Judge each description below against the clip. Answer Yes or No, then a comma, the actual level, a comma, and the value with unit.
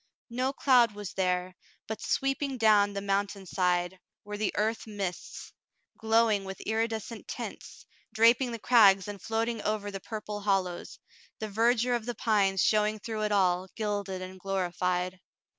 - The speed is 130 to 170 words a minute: Yes, average, 150 wpm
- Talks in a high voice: Yes, high, 210 Hz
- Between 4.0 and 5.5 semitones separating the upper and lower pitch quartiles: No, average, 2.7 semitones